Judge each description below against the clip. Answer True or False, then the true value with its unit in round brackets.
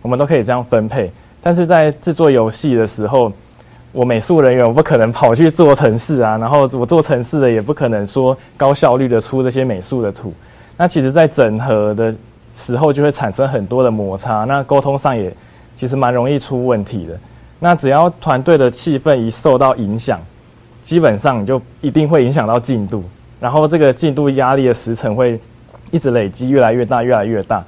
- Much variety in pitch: False (4.0 semitones)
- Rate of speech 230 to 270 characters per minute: False (300 characters per minute)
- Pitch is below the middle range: True (125 Hz)